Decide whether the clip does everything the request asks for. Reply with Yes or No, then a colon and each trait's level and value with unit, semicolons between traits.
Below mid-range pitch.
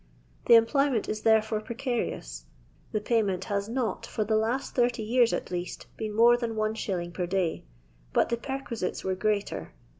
No: high, 220 Hz